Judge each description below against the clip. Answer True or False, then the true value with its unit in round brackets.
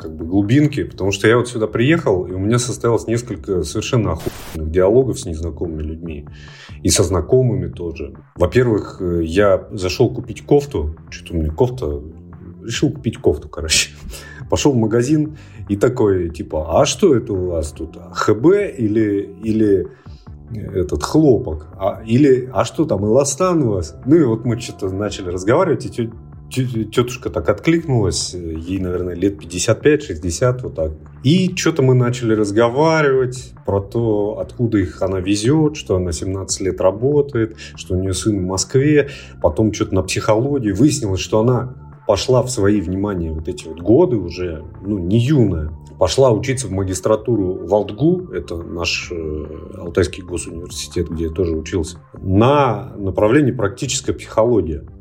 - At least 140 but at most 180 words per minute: True (150 wpm)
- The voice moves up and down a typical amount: False (5.9 semitones)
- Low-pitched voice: True (100 Hz)